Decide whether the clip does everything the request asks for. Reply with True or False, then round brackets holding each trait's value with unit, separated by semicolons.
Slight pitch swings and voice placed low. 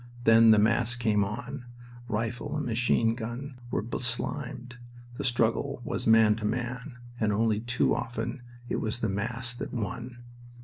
True (1.9 semitones; 115 Hz)